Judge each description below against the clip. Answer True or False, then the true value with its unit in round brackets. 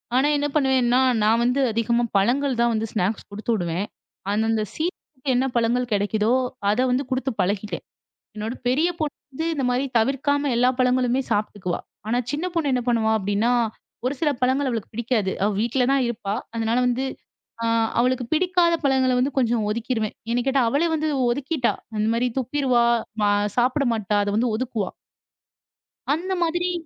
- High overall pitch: True (245 Hz)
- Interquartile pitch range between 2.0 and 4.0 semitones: True (3.6 semitones)